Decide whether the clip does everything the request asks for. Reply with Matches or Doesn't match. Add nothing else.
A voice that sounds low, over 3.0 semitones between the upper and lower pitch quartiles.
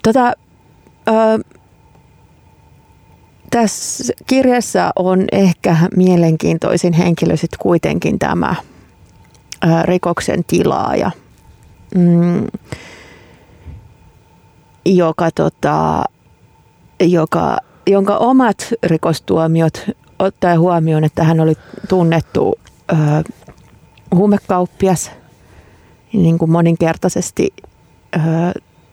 Doesn't match